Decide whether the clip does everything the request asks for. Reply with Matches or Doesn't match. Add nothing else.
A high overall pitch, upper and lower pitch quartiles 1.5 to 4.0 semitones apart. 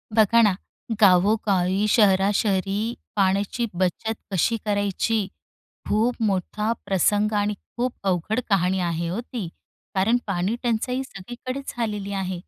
Matches